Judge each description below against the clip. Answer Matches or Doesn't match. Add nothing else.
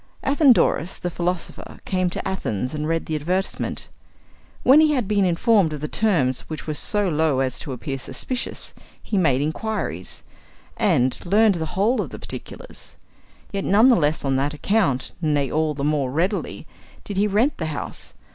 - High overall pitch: Doesn't match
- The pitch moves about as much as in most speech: Doesn't match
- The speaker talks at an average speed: Matches